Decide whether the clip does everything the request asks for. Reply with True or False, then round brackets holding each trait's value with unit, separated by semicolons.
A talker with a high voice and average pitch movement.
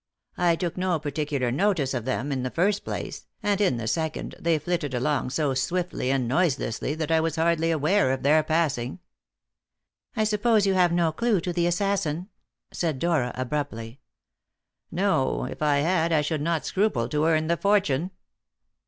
False (160 Hz; 4.3 semitones)